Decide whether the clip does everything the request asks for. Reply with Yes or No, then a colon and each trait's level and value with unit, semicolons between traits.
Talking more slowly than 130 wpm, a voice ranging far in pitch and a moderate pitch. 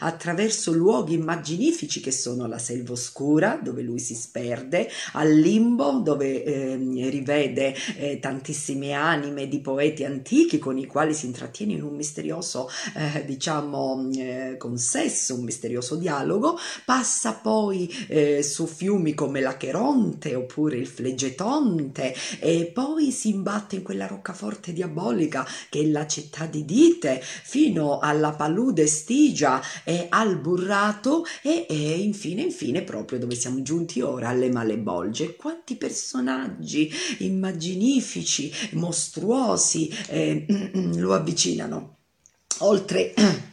Yes: average, 120 wpm; wide, 7.3 semitones; medium, 155 Hz